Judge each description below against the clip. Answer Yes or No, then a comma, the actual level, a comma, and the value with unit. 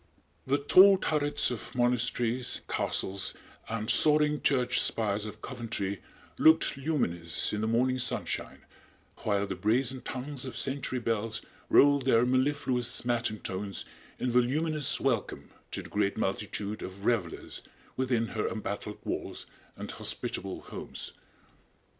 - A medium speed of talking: No, slow, 125 wpm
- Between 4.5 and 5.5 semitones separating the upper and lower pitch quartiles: No, average, 4.0 semitones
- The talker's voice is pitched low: Yes, low, 120 Hz